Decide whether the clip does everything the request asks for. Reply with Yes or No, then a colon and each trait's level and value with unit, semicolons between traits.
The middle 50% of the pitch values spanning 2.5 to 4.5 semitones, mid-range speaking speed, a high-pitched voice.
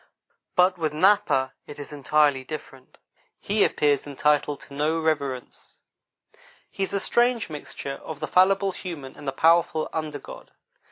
No: average, 4.2 semitones; average, 150 wpm; medium, 150 Hz